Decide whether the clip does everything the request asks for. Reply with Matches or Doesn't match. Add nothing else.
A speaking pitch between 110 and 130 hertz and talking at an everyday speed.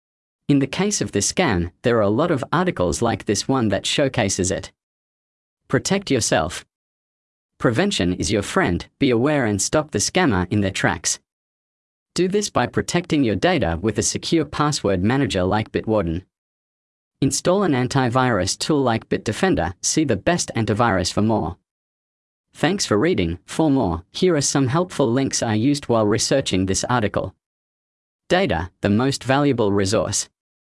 Matches